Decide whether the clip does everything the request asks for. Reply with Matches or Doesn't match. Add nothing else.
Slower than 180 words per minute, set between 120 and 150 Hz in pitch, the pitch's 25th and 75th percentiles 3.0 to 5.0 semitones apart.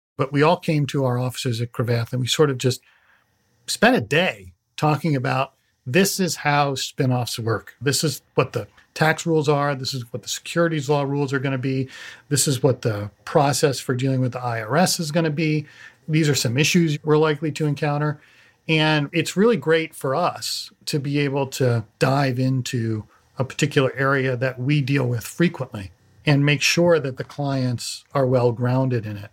Doesn't match